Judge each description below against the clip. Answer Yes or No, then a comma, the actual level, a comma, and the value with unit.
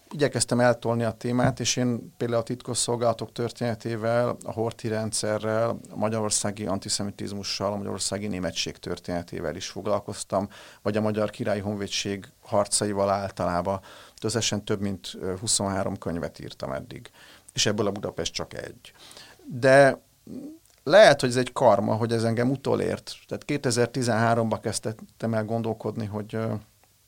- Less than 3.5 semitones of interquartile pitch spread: Yes, average, 2.8 semitones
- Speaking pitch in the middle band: No, low, 110 Hz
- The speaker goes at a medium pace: Yes, average, 130 wpm